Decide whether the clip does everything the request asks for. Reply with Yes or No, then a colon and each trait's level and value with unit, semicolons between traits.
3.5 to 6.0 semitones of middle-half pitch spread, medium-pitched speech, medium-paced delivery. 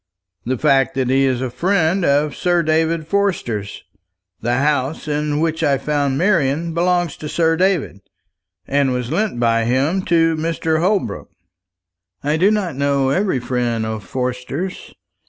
Yes: average, 4.5 semitones; medium, 150 Hz; average, 150 wpm